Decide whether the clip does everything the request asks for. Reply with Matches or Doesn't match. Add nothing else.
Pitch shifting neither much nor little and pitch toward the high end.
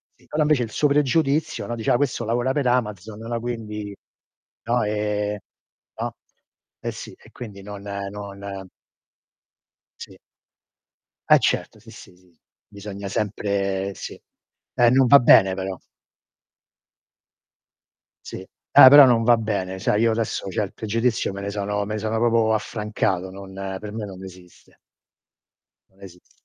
Doesn't match